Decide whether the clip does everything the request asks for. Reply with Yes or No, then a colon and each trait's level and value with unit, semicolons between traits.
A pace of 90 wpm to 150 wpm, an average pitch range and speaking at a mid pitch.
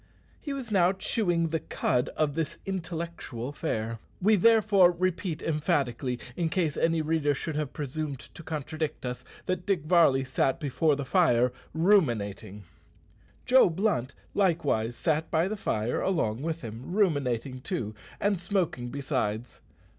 No: average, 140 wpm; wide, 5.7 semitones; medium, 155 Hz